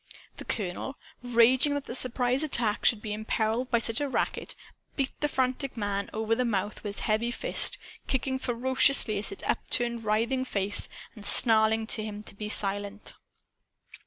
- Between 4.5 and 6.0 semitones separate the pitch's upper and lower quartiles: No, average, 3.2 semitones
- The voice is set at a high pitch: Yes, high, 230 Hz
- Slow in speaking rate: No, average, 165 wpm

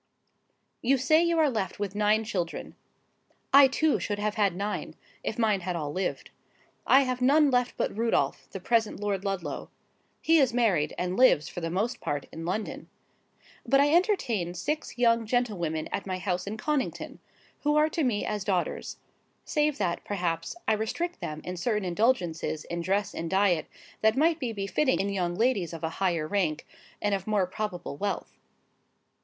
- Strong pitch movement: Yes, wide, 5.9 semitones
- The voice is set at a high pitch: Yes, high, 205 Hz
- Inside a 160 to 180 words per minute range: Yes, average, 175 wpm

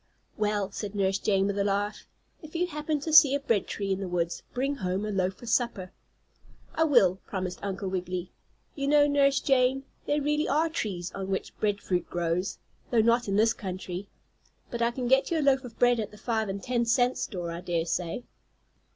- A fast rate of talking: Yes, fast, 210 wpm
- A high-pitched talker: Yes, high, 210 Hz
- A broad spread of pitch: Yes, wide, 5.8 semitones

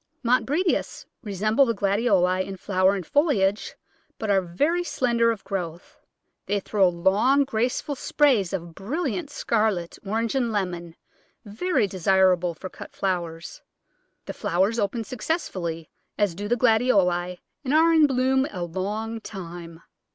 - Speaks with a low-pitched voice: No, high, 205 Hz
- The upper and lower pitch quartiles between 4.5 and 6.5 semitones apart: Yes, average, 5.3 semitones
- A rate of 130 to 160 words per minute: Yes, slow, 135 wpm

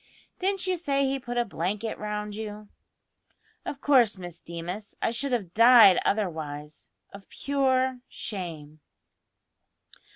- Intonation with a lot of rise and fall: Yes, wide, 6.3 semitones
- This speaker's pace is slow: Yes, slow, 125 wpm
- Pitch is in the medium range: No, high, 215 Hz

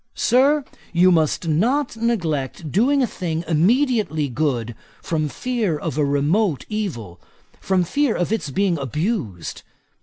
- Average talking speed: No, slow, 125 wpm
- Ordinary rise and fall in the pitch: No, wide, 7.3 semitones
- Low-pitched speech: No, medium, 175 Hz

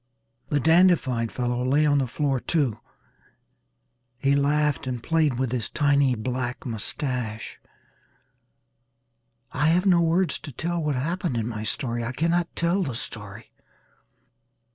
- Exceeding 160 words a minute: No, slow, 135 wpm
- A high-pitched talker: No, medium, 140 Hz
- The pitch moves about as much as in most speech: Yes, average, 4.9 semitones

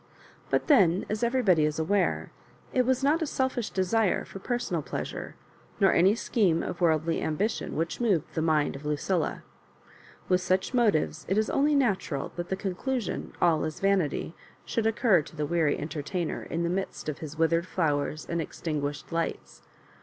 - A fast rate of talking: No, average, 175 wpm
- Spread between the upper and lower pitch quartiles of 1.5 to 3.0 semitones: No, average, 5.3 semitones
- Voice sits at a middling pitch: Yes, medium, 180 Hz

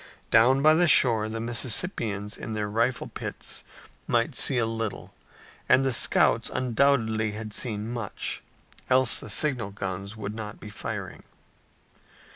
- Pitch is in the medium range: No, low, 115 Hz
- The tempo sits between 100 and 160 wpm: Yes, average, 140 wpm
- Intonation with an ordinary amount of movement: Yes, average, 3.3 semitones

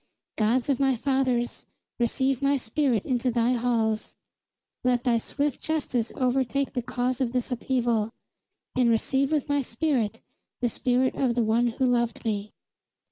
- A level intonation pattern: Yes, narrow, 2.3 semitones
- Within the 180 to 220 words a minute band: No, average, 150 wpm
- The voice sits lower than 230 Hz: No, high, 245 Hz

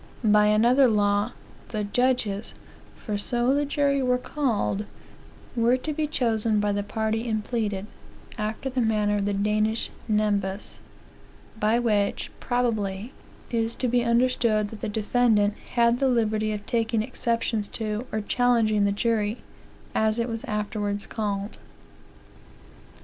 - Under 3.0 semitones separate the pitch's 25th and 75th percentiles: Yes, narrow, 2.6 semitones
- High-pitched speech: Yes, high, 220 Hz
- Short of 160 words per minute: Yes, average, 140 wpm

